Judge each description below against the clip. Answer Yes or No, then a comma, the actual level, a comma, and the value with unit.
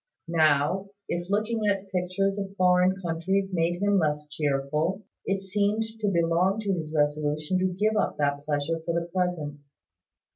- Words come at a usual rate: Yes, average, 155 wpm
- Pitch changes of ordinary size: Yes, average, 4.2 semitones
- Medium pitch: Yes, medium, 180 Hz